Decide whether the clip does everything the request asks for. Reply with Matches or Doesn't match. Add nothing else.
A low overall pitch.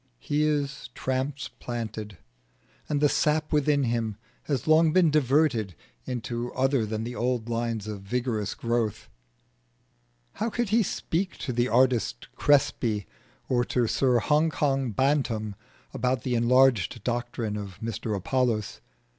Matches